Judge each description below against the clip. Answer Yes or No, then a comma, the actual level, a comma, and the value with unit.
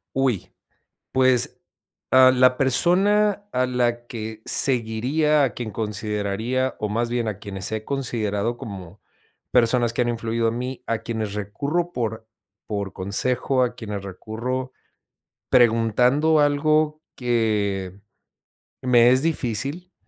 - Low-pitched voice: Yes, low, 120 Hz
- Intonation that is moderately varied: Yes, average, 3.2 semitones